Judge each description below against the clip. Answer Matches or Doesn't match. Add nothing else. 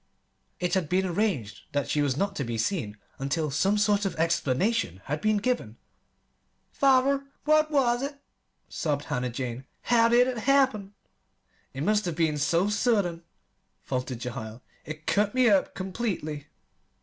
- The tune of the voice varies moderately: Doesn't match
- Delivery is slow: Doesn't match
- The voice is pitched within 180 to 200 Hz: Matches